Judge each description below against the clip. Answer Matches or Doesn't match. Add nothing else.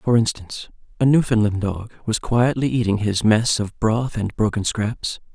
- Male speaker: Matches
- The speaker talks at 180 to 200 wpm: Doesn't match